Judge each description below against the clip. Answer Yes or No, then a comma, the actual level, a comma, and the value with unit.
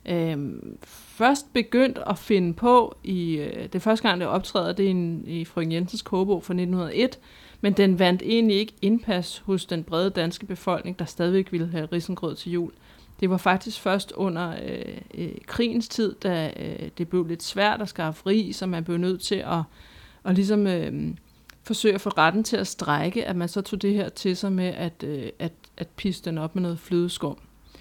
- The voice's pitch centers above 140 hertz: Yes, medium, 185 Hz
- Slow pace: No, average, 205 wpm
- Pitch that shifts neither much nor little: Yes, average, 3.0 semitones